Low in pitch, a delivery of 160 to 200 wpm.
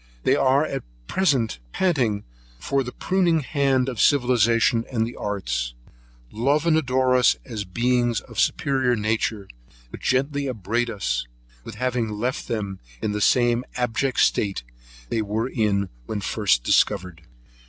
No: low, 120 Hz; average, 140 wpm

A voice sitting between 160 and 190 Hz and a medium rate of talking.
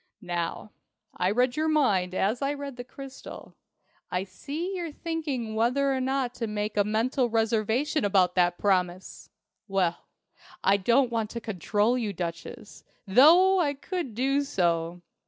No: high, 230 Hz; average, 150 wpm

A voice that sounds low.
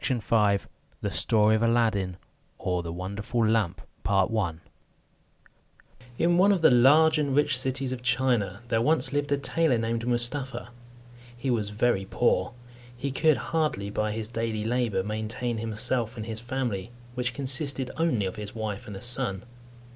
Yes: low, 120 Hz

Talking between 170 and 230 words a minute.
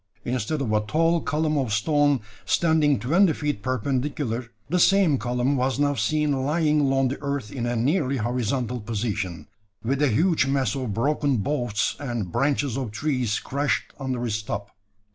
No: average, 160 wpm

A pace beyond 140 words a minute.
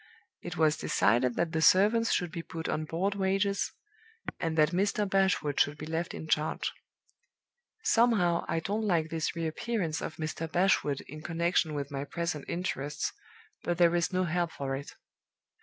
Yes: average, 170 wpm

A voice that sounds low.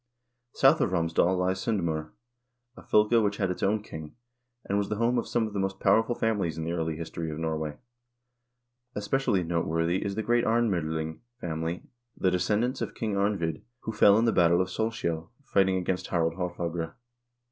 Yes: very low, 95 Hz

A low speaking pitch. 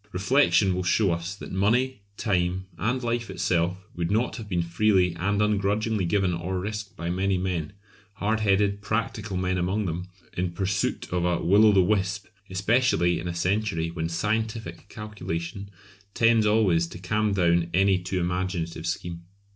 Yes: very low, 95 Hz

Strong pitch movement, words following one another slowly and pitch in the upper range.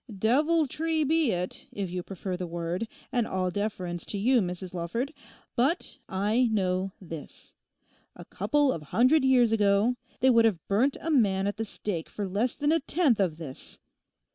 No: wide, 6.1 semitones; average, 165 wpm; high, 210 Hz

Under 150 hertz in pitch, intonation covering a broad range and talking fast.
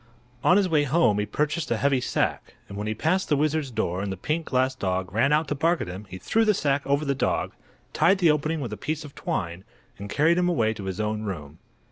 Yes: medium, 140 Hz; wide, 7.2 semitones; fast, 250 wpm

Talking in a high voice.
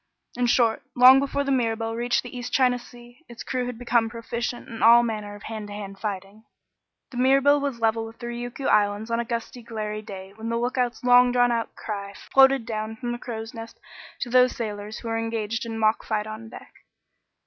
Yes: high, 230 Hz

